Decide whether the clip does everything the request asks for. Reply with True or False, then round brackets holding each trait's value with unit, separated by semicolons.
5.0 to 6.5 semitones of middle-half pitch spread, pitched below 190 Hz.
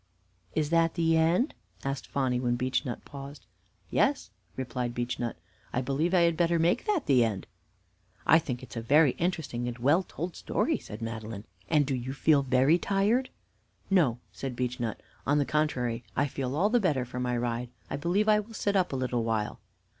True (5.3 semitones; 135 Hz)